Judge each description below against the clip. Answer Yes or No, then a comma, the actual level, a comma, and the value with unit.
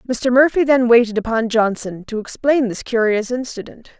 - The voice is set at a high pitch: Yes, high, 235 Hz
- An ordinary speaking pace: Yes, average, 165 wpm